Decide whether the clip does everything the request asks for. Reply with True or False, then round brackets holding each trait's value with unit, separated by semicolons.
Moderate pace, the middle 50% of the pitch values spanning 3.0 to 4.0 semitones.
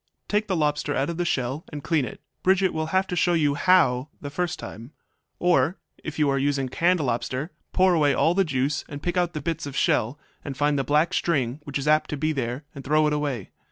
False (235 wpm; 3.7 semitones)